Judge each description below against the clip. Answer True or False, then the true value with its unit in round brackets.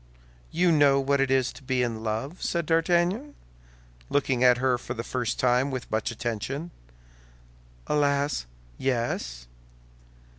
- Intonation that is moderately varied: True (3.4 semitones)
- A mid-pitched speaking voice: False (130 Hz)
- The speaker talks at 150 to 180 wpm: False (135 wpm)